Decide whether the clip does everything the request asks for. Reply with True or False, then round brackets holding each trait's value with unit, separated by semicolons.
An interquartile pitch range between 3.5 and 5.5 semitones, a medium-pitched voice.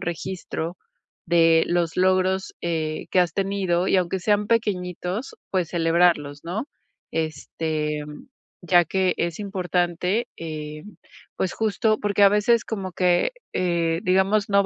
False (2.8 semitones; 180 Hz)